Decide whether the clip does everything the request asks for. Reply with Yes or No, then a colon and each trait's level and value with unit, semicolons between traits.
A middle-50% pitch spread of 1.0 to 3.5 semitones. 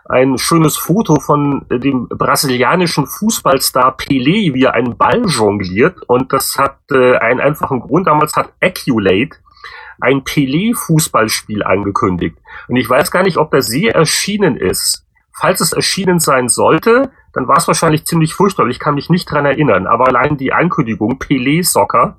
No: average, 4.3 semitones